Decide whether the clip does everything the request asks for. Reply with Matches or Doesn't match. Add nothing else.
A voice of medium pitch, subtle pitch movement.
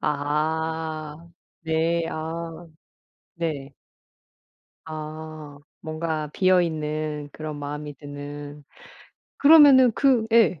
Matches